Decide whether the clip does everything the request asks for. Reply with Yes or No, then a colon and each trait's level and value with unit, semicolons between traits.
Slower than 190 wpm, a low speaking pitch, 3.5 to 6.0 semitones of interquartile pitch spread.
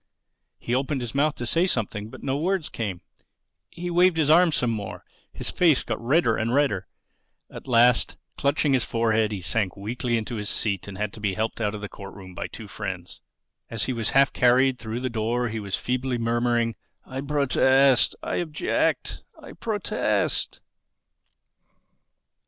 Yes: average, 170 wpm; low, 120 Hz; average, 4.2 semitones